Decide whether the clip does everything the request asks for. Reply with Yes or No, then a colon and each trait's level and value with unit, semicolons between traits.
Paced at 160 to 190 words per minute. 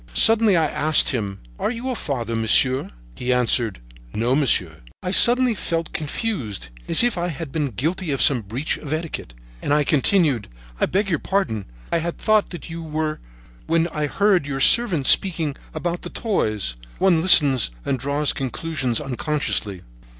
Yes: average, 165 wpm